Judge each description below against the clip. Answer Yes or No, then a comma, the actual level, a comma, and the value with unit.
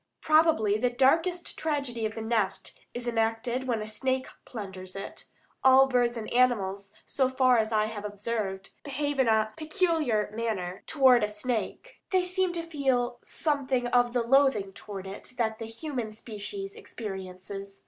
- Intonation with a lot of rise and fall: No, average, 4.1 semitones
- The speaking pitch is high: Yes, high, 240 Hz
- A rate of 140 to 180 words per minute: Yes, average, 155 wpm